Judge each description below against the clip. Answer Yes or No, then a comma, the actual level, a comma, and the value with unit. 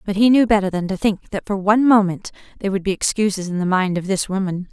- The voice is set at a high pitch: Yes, high, 195 Hz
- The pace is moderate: No, fast, 265 wpm